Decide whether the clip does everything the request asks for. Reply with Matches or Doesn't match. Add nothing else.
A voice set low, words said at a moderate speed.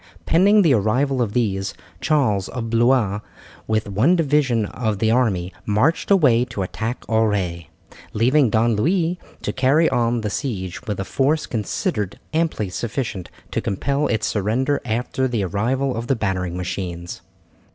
Matches